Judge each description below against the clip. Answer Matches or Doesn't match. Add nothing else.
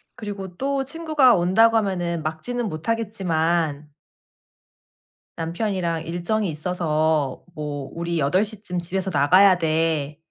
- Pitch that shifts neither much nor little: Matches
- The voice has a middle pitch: Matches